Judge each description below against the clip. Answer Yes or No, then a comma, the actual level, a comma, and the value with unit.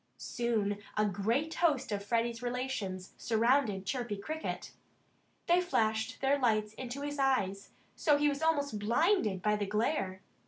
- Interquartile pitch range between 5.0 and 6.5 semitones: Yes, wide, 5.4 semitones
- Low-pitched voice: No, high, 235 Hz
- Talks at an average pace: Yes, average, 150 wpm